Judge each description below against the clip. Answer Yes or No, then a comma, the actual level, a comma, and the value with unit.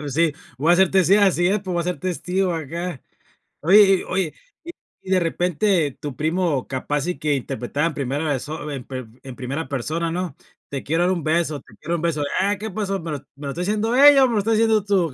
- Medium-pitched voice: Yes, medium, 170 Hz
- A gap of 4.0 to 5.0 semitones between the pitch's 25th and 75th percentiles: Yes, average, 4.5 semitones